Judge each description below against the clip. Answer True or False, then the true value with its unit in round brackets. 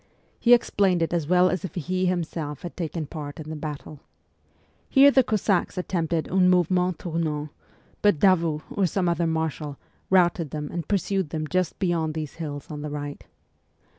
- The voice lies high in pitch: False (170 Hz)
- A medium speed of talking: True (170 wpm)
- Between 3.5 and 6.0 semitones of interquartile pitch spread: False (3.1 semitones)